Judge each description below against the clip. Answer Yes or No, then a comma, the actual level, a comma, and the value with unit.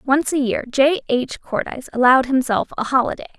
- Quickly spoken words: No, average, 175 wpm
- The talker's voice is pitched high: Yes, very high, 260 Hz